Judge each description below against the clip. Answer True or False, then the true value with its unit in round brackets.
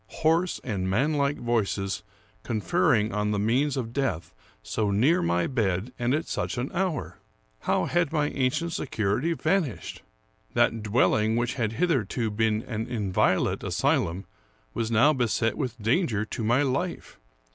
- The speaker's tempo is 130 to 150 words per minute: True (145 wpm)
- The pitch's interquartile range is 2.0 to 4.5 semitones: False (5.0 semitones)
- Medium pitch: False (120 Hz)